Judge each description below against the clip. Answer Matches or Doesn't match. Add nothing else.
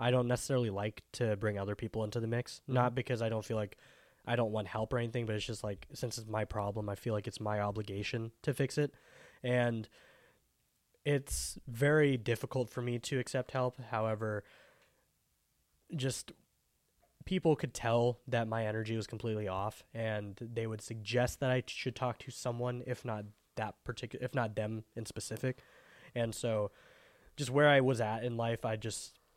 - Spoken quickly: Doesn't match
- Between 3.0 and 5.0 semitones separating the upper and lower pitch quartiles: Doesn't match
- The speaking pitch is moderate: Doesn't match